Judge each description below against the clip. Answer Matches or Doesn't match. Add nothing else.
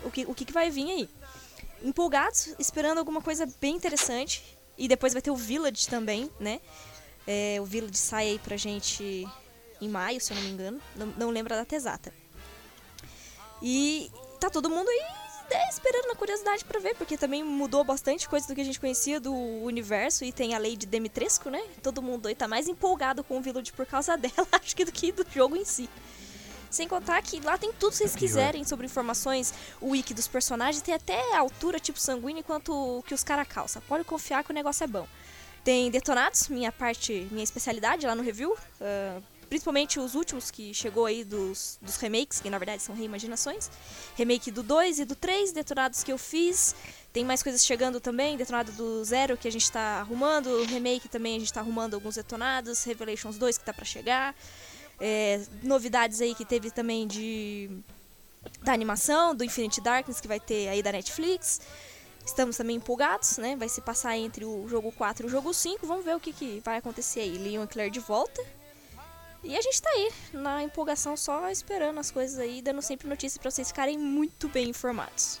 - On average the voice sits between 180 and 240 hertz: Doesn't match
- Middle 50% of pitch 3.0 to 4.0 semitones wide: Doesn't match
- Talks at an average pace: Doesn't match